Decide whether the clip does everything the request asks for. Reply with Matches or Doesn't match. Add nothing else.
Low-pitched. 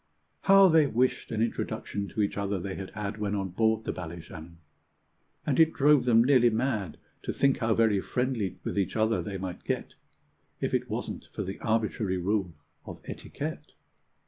Matches